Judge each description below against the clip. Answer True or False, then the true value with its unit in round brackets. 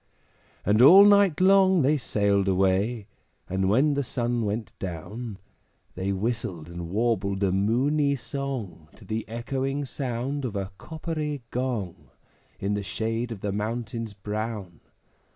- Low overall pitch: True (115 Hz)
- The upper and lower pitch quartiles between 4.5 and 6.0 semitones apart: True (5.4 semitones)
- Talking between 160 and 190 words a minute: False (135 wpm)